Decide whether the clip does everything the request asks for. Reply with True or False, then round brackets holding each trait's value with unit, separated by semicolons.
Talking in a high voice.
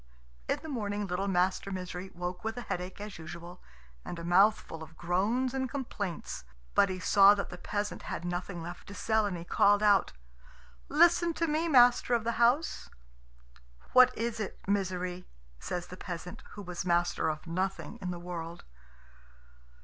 True (195 Hz)